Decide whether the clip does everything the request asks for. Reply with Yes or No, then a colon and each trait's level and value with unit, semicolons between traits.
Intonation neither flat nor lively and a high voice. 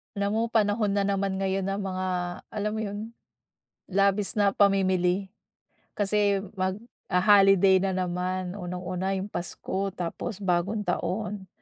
No: narrow, 1.6 semitones; high, 195 Hz